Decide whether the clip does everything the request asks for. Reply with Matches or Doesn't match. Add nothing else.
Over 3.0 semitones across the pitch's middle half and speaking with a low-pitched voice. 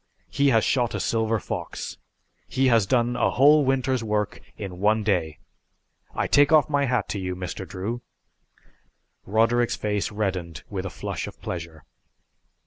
Matches